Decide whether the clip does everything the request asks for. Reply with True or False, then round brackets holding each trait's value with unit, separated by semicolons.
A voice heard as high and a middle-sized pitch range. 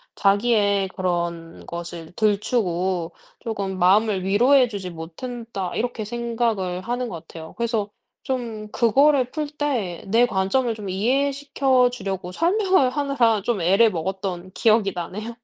True (215 Hz; 4.7 semitones)